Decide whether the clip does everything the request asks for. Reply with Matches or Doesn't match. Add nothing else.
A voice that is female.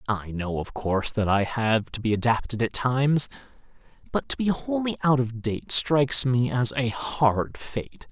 Doesn't match